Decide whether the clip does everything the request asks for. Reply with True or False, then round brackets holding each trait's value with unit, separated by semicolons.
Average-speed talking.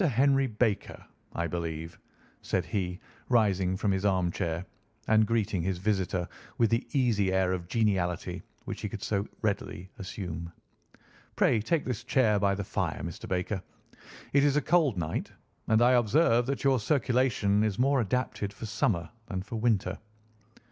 True (155 wpm)